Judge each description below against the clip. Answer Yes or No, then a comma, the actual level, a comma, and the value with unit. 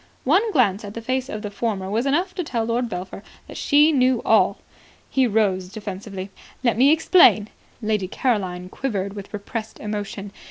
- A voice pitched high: Yes, high, 220 Hz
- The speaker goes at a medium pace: Yes, average, 170 wpm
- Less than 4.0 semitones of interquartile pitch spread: No, average, 4.4 semitones